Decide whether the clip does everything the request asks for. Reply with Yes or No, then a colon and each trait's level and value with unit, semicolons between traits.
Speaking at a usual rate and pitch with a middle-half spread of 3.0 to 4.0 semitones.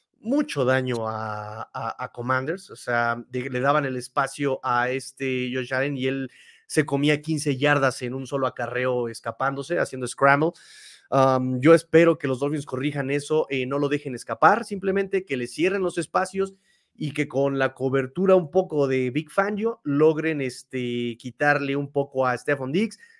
Yes: average, 175 wpm; average, 3.6 semitones